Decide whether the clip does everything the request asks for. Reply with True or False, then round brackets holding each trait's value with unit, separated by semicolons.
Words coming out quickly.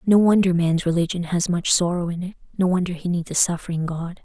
True (225 wpm)